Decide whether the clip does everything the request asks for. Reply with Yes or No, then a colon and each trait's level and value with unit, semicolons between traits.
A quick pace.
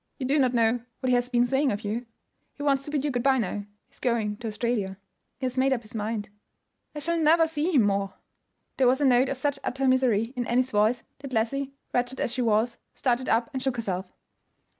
Yes: fast, 235 wpm